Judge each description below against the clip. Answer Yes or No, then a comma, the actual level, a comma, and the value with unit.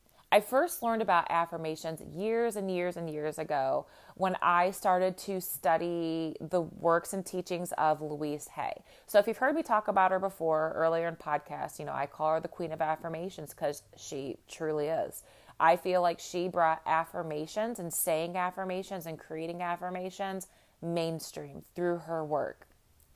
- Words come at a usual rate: Yes, average, 165 wpm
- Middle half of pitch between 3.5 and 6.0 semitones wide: No, average, 2.7 semitones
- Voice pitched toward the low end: No, medium, 170 Hz